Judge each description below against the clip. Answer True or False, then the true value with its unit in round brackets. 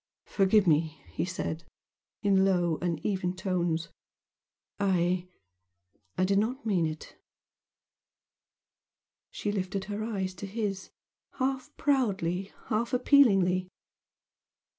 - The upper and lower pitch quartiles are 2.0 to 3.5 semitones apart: True (3.0 semitones)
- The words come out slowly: True (95 wpm)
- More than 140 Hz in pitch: True (190 Hz)